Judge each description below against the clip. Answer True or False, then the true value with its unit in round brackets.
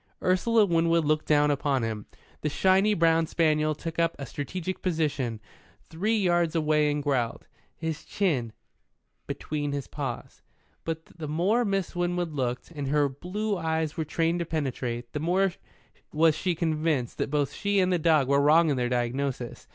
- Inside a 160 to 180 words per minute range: True (165 wpm)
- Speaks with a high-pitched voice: False (155 Hz)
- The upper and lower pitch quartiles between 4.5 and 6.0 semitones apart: False (3.4 semitones)